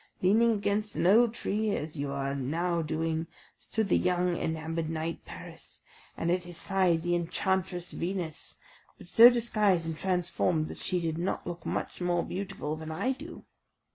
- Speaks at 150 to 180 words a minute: Yes, average, 170 wpm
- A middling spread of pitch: Yes, average, 3.3 semitones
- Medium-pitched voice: Yes, medium, 175 Hz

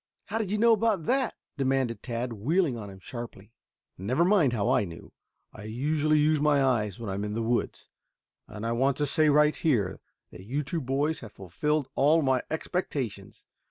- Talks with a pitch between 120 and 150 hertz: Yes, low, 135 Hz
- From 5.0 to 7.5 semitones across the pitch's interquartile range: Yes, wide, 5.5 semitones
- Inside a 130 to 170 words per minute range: No, average, 195 wpm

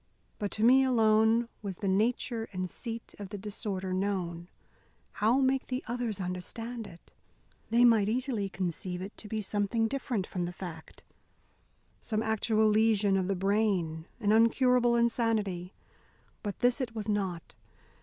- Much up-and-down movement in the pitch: No, average, 3.4 semitones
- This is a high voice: Yes, high, 215 Hz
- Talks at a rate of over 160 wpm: No, average, 150 wpm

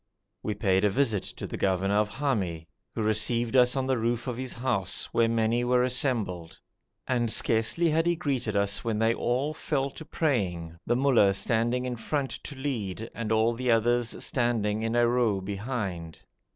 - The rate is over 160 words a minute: Yes, average, 180 wpm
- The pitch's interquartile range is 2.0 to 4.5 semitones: Yes, average, 3.5 semitones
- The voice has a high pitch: No, low, 115 Hz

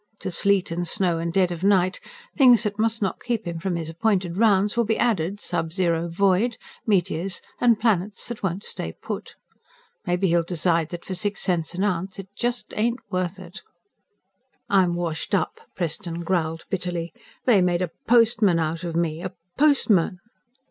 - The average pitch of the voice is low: No, medium, 185 Hz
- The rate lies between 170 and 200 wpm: Yes, average, 175 wpm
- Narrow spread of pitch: No, average, 3.5 semitones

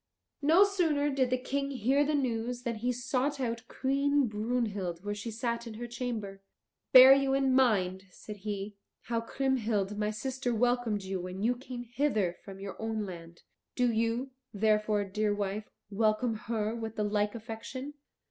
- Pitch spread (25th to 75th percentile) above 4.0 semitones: No, average, 3.7 semitones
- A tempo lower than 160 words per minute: No, average, 165 wpm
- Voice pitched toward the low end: No, high, 230 Hz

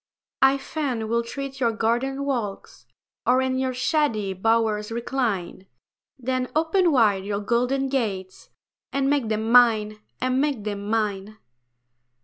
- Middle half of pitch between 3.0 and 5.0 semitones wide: Yes, average, 4.0 semitones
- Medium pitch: No, high, 235 Hz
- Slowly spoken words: Yes, slow, 130 wpm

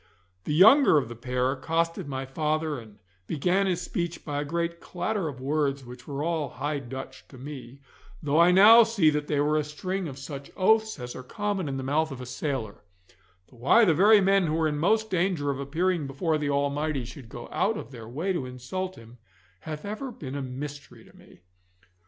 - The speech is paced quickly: Yes, fast, 210 wpm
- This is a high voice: No, medium, 150 Hz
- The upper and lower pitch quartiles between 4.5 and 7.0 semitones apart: Yes, average, 4.9 semitones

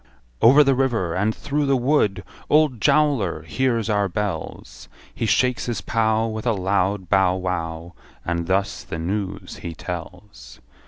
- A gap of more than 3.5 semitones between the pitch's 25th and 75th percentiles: Yes, average, 5.2 semitones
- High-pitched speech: No, low, 105 Hz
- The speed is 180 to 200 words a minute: No, average, 150 wpm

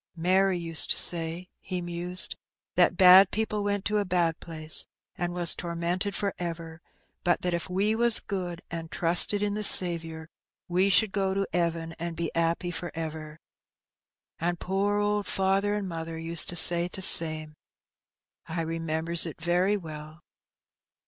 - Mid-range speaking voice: Yes, medium, 175 Hz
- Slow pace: No, average, 160 wpm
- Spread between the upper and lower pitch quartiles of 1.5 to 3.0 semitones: Yes, average, 2.7 semitones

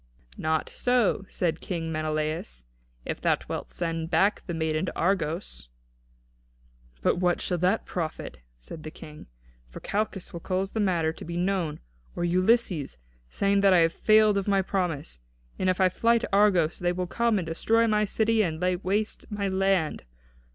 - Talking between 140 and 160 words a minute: No, average, 170 wpm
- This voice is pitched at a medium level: Yes, medium, 180 Hz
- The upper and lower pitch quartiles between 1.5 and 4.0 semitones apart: Yes, average, 3.6 semitones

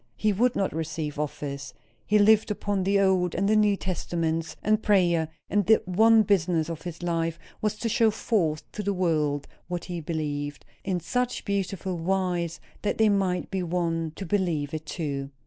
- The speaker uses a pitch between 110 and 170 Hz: No, medium, 180 Hz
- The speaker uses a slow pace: No, average, 175 wpm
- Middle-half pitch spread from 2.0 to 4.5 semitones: Yes, average, 3.8 semitones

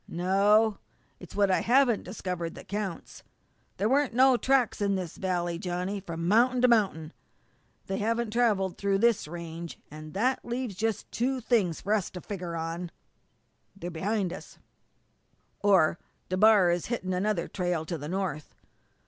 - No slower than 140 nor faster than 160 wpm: Yes, average, 155 wpm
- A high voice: Yes, high, 195 Hz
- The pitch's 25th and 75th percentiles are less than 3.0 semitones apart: No, average, 4.2 semitones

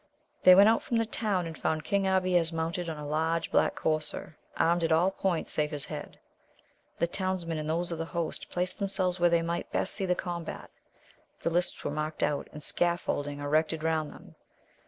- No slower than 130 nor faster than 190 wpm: No, average, 200 wpm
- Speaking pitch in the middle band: Yes, medium, 170 Hz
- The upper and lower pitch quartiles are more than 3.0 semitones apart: No, narrow, 2.5 semitones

